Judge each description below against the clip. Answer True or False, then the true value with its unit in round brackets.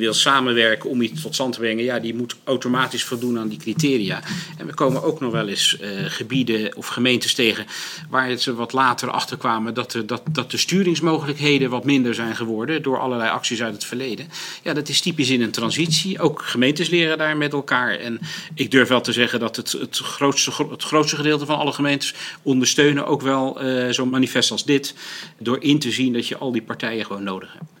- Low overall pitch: True (130 Hz)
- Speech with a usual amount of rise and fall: True (3.7 semitones)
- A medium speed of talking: False (215 wpm)